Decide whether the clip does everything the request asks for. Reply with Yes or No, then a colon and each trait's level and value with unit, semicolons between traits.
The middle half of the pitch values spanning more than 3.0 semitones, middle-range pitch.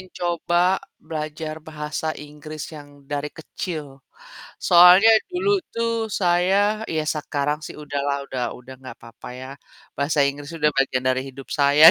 Yes: average, 3.7 semitones; medium, 150 Hz